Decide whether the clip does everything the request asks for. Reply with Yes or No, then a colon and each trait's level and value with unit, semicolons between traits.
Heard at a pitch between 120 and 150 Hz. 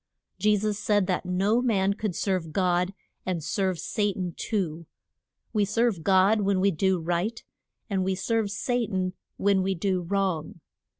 No: high, 195 Hz